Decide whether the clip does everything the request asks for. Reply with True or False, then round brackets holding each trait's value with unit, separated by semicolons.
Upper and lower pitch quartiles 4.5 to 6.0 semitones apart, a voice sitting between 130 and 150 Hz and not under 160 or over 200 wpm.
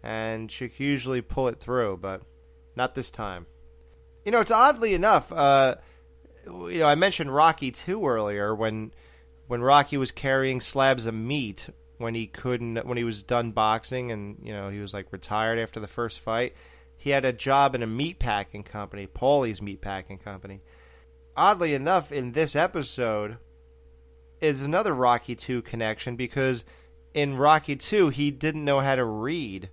False (5.5 semitones; 115 Hz; 170 wpm)